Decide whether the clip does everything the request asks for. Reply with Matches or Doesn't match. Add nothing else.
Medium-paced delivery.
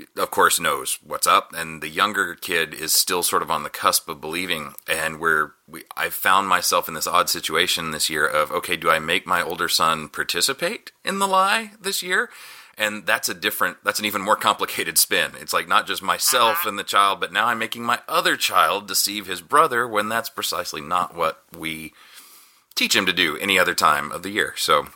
Doesn't match